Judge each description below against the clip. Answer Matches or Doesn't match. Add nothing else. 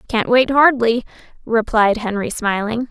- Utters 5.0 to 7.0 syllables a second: Doesn't match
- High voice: Matches